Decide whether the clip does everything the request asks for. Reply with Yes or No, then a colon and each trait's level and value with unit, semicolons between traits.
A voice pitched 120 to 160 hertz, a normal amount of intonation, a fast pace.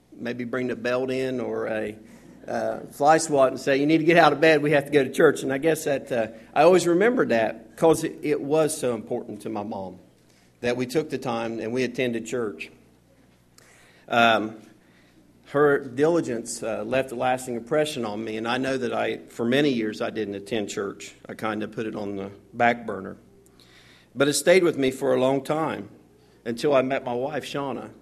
Yes: low, 125 Hz; average, 4.4 semitones; fast, 210 wpm